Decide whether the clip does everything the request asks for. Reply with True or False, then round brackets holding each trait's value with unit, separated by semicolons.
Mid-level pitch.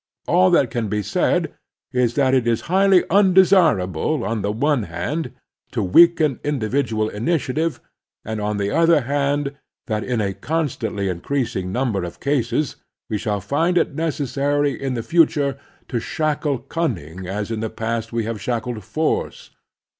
False (125 Hz)